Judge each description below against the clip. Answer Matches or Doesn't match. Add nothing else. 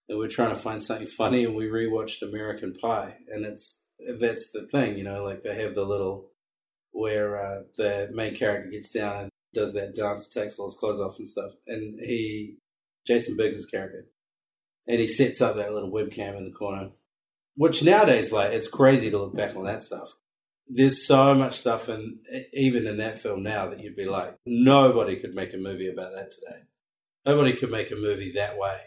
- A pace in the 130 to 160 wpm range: Doesn't match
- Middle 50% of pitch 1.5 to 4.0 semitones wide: Matches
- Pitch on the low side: Matches